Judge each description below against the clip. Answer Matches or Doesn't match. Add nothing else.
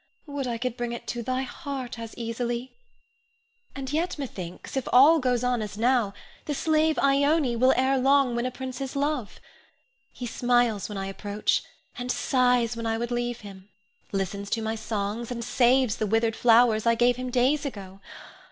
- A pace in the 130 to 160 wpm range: Doesn't match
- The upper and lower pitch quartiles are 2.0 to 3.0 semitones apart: Matches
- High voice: Matches